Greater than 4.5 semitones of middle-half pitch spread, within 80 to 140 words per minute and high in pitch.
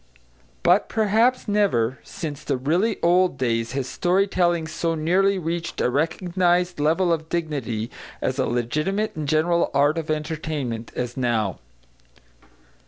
No: average, 5.0 semitones; slow, 135 wpm; medium, 160 Hz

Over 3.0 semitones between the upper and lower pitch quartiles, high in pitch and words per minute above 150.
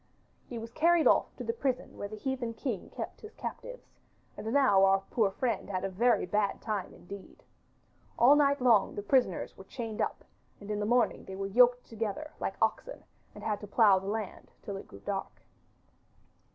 Yes: average, 4.2 semitones; high, 220 Hz; average, 190 wpm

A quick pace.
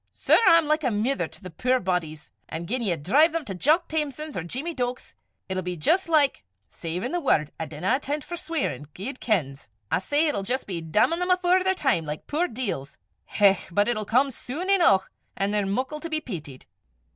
Yes: fast, 215 wpm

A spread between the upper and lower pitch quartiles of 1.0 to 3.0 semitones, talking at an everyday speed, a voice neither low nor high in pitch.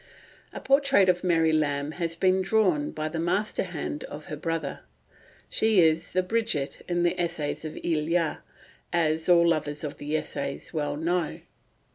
Yes: average, 2.7 semitones; average, 160 wpm; medium, 165 Hz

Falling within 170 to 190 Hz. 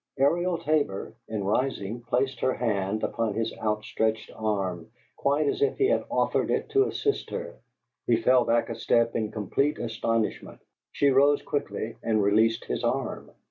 No: low, 115 Hz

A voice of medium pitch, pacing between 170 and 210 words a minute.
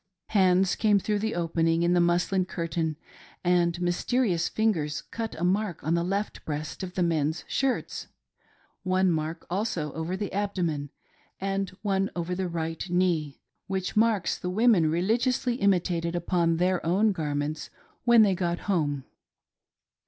No: medium, 180 Hz; average, 155 wpm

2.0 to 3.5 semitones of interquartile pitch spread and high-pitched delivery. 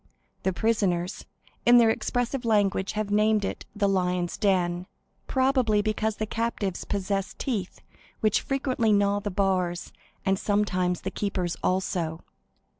Yes: average, 2.9 semitones; high, 200 Hz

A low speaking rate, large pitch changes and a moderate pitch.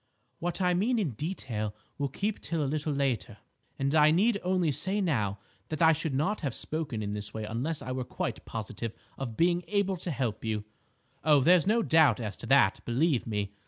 No: average, 200 wpm; wide, 7.2 semitones; medium, 150 Hz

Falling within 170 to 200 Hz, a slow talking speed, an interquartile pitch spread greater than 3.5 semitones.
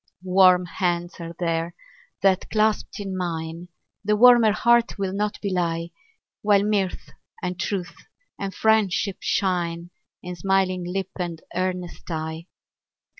No: medium, 185 Hz; slow, 125 wpm; narrow, 2.5 semitones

